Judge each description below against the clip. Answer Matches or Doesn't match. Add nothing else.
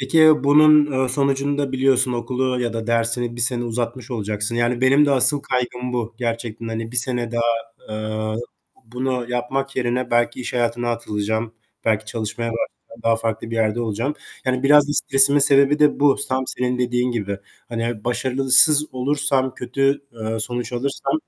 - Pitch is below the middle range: Matches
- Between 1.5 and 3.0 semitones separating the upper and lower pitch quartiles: Matches